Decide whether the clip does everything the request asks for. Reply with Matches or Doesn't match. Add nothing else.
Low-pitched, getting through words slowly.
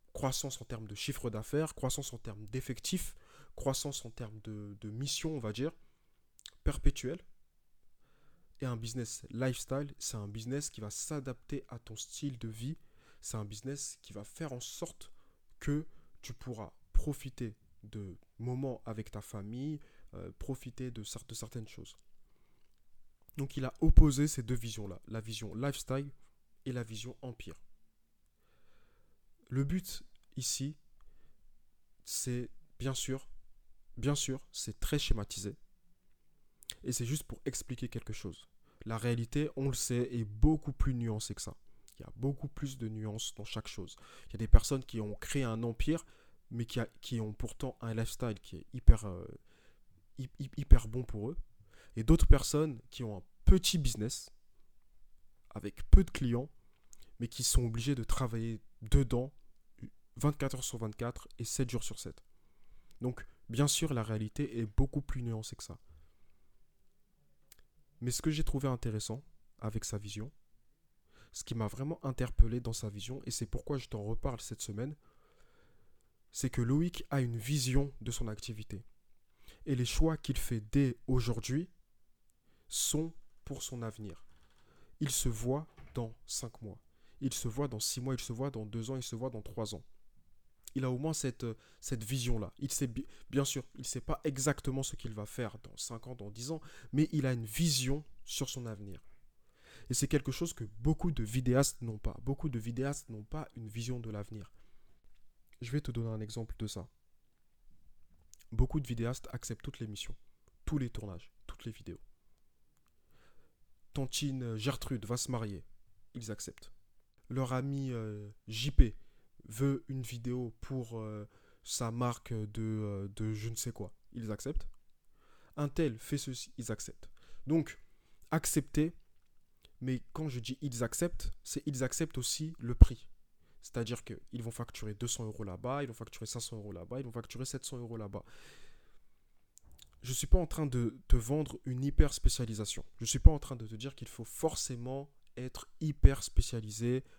Doesn't match